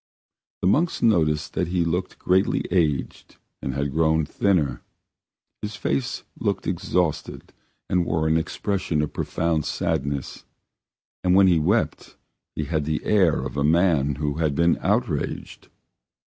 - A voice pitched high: No, very low, 85 Hz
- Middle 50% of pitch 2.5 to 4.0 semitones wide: Yes, average, 3.7 semitones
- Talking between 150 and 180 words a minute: No, average, 140 wpm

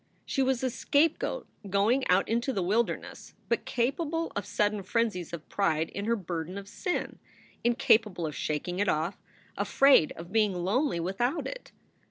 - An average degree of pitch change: No, wide, 5.9 semitones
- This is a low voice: No, high, 205 Hz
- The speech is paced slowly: No, average, 160 wpm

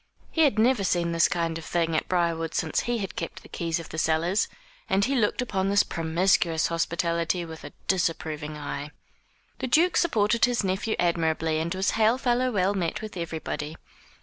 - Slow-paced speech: No, average, 185 wpm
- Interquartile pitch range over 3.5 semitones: Yes, average, 4.4 semitones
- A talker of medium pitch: Yes, medium, 175 Hz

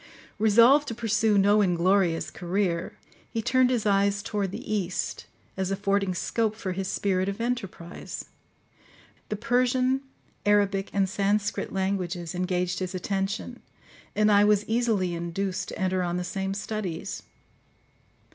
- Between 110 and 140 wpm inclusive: Yes, slow, 135 wpm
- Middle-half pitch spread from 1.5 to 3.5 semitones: Yes, narrow, 2.5 semitones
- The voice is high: Yes, high, 200 Hz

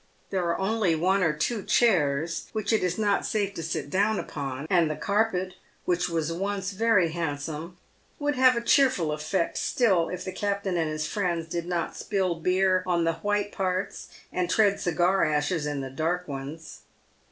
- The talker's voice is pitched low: No, medium, 180 Hz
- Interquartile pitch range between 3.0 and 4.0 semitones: Yes, average, 3.7 semitones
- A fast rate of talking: No, average, 180 wpm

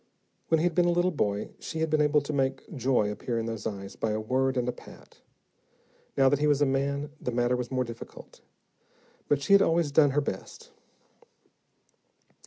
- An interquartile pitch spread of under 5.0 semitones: Yes, average, 3.8 semitones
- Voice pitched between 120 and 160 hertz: Yes, low, 135 Hz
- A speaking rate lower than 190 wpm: No, average, 200 wpm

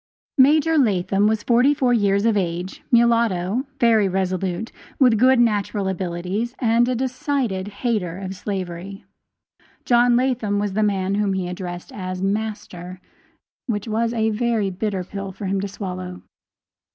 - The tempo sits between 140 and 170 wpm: Yes, average, 145 wpm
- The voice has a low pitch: No, high, 205 Hz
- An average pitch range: Yes, average, 3.9 semitones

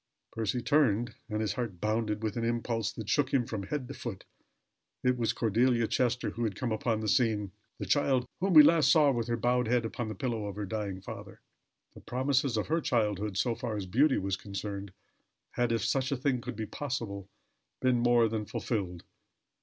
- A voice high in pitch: No, low, 115 Hz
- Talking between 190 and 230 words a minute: Yes, average, 200 wpm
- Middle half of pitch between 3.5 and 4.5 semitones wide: No, average, 3.0 semitones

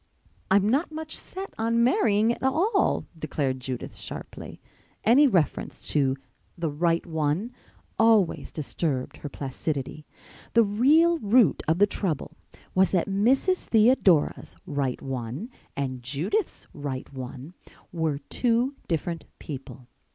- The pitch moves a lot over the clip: Yes, wide, 8.6 semitones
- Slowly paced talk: Yes, slow, 120 wpm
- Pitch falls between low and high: Yes, medium, 175 Hz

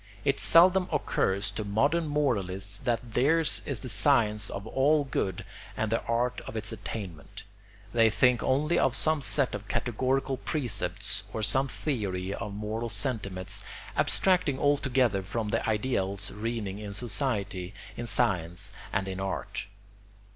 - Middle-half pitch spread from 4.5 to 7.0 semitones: Yes, average, 5.0 semitones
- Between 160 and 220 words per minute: No, average, 140 wpm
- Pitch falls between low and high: No, low, 115 Hz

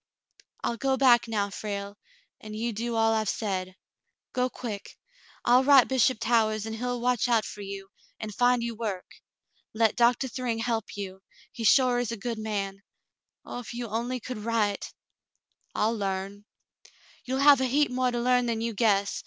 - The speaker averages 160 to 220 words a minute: Yes, average, 180 wpm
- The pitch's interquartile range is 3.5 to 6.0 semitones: No, average, 2.9 semitones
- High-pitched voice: Yes, high, 230 Hz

